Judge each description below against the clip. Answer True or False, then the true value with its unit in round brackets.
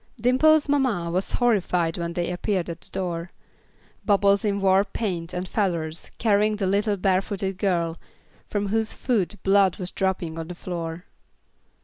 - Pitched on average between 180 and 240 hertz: True (190 Hz)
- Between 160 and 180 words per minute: False (150 wpm)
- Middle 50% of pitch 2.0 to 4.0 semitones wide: True (3.1 semitones)